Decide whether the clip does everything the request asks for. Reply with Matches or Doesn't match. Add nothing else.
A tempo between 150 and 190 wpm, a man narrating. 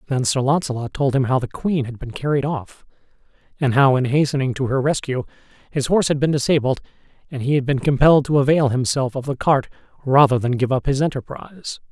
Doesn't match